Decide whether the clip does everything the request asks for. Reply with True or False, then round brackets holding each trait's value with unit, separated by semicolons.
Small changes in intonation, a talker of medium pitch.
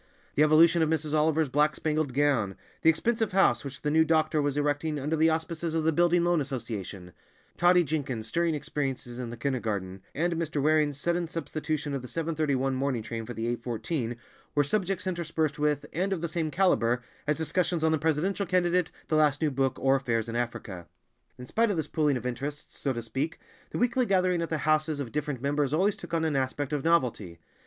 False (3.7 semitones; 150 Hz)